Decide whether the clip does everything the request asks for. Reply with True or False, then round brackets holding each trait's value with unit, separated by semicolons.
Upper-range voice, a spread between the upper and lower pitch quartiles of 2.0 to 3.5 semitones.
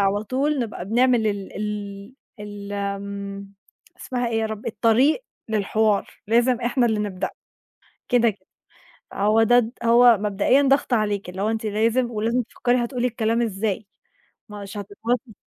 True (220 Hz; 2.9 semitones)